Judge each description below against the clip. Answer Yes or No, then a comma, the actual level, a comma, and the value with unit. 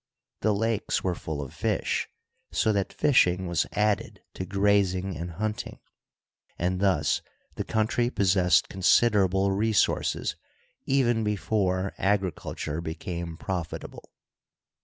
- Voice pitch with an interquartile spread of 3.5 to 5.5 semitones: No, average, 3.0 semitones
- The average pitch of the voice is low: Yes, very low, 95 Hz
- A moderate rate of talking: No, slow, 110 wpm